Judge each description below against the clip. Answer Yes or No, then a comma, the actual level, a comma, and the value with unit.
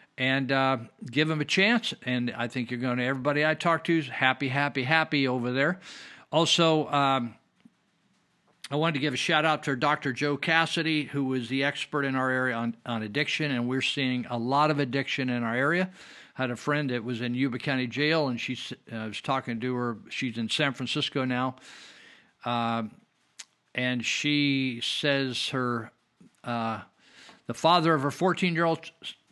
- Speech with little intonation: No, average, 3.4 semitones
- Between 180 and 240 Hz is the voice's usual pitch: No, low, 135 Hz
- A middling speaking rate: Yes, average, 185 wpm